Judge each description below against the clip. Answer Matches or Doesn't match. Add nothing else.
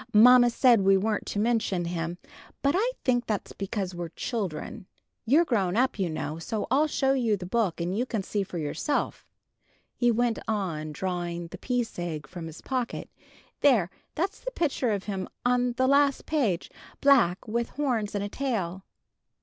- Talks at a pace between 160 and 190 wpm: Matches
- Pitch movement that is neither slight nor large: Doesn't match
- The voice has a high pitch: Matches